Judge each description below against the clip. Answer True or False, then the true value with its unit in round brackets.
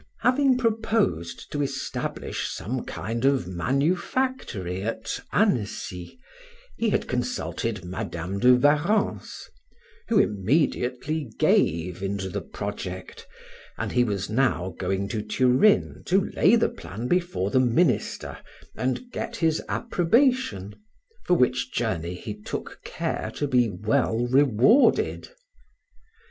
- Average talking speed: False (115 wpm)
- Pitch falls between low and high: False (125 Hz)